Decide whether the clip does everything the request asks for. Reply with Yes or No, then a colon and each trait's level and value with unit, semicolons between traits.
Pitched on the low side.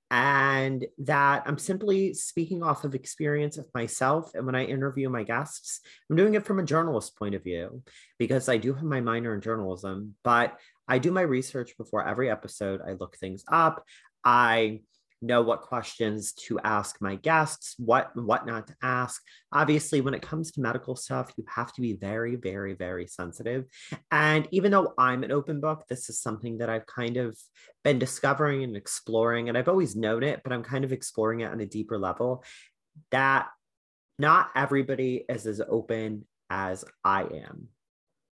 Yes: low, 125 Hz